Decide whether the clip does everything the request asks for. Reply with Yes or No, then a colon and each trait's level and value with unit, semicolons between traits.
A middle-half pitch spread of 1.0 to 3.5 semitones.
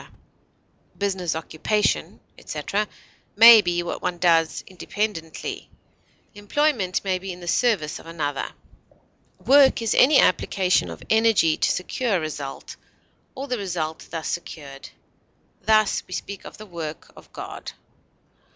No: average, 4.7 semitones